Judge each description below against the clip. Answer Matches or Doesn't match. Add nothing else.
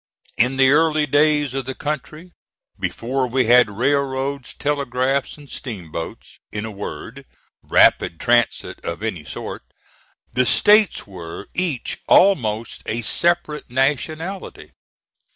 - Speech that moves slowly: Matches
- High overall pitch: Doesn't match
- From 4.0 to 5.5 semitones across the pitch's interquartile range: Matches